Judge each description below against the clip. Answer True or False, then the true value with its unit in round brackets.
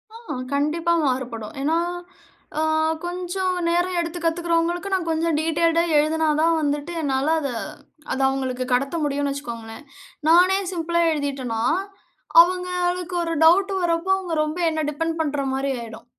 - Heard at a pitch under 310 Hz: False (325 Hz)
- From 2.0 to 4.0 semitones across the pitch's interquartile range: True (3.7 semitones)